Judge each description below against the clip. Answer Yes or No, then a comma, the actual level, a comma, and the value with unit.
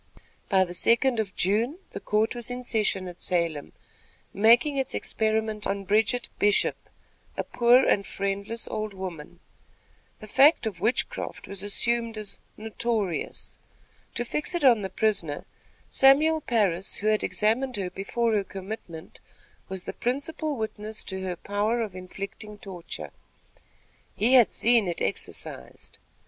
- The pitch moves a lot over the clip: No, average, 3.6 semitones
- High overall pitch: Yes, high, 215 Hz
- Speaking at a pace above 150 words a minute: No, average, 140 wpm